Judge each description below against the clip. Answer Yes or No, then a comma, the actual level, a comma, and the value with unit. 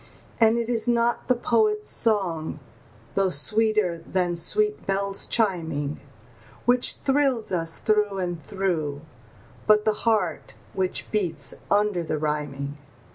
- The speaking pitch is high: Yes, high, 195 Hz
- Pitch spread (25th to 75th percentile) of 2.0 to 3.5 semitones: No, average, 5.2 semitones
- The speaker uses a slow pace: Yes, slow, 125 wpm